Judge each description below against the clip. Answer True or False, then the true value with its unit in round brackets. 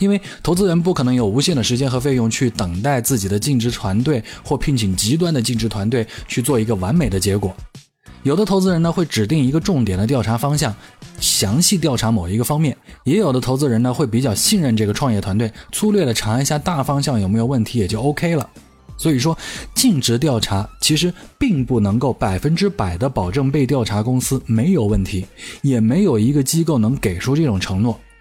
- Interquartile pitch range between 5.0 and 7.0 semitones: True (5.3 semitones)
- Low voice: True (125 Hz)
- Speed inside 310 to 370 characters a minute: True (325 characters per minute)